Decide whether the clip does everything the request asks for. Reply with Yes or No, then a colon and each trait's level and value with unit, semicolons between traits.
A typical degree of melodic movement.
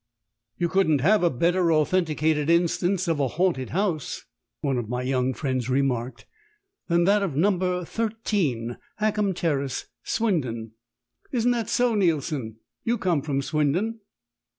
No: wide, 6.2 semitones